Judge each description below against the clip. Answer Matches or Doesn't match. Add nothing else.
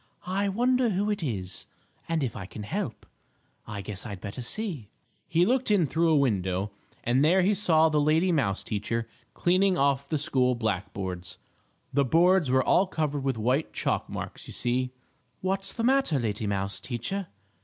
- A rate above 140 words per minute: Matches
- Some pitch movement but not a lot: Doesn't match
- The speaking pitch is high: Doesn't match